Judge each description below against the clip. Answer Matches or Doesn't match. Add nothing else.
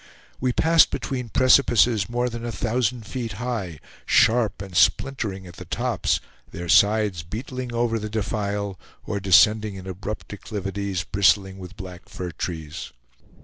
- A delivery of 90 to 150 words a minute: Matches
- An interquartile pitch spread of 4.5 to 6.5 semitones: Doesn't match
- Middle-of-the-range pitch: Doesn't match